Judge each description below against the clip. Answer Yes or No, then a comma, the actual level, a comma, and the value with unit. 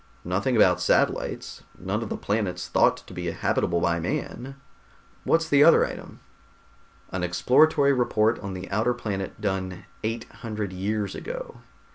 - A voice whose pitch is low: Yes, low, 105 Hz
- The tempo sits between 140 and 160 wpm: Yes, average, 145 wpm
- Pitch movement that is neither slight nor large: Yes, average, 4.8 semitones